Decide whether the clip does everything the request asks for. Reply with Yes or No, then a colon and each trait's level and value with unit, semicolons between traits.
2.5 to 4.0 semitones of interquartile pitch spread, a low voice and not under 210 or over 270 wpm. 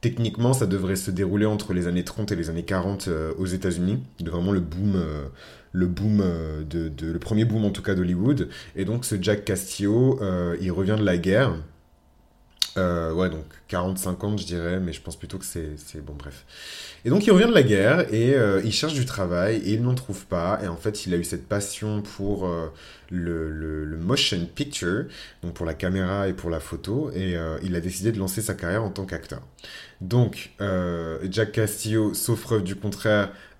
Yes: average, 3.6 semitones; very low, 95 Hz; average, 215 wpm